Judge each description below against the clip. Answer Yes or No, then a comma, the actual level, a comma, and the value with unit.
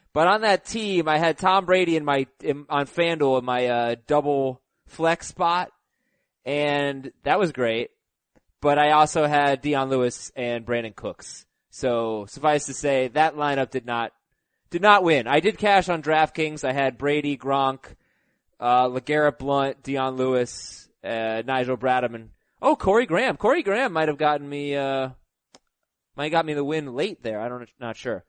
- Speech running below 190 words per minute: Yes, average, 175 wpm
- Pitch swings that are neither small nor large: Yes, average, 3.3 semitones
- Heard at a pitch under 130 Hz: No, medium, 140 Hz